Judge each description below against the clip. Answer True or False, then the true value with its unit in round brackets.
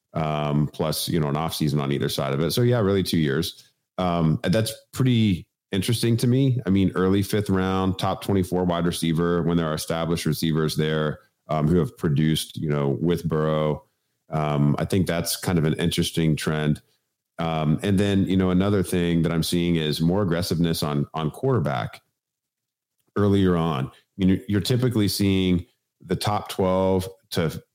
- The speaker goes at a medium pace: True (180 wpm)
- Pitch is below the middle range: True (85 Hz)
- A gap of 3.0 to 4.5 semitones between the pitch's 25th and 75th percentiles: True (3.6 semitones)